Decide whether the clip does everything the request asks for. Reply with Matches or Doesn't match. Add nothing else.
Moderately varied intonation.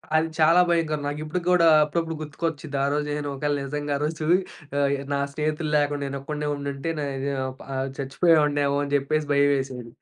Doesn't match